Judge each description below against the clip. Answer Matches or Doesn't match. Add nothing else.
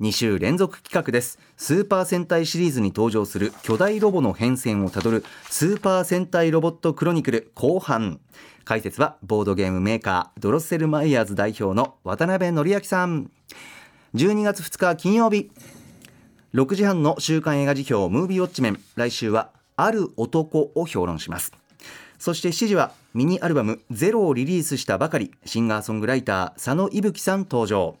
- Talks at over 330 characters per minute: Matches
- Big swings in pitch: Matches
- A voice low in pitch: Doesn't match